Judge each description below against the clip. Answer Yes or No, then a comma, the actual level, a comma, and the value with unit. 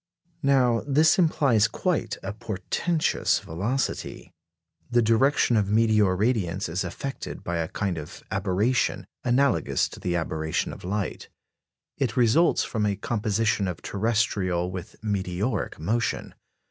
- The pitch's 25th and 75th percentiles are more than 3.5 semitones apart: Yes, average, 4.7 semitones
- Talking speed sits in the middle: No, slow, 125 wpm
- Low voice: Yes, low, 105 Hz